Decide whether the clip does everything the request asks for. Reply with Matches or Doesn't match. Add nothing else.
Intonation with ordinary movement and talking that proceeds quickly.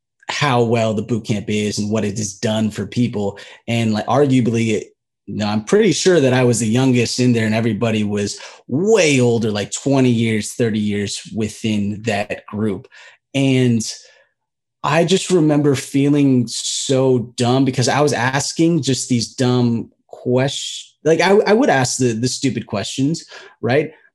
Doesn't match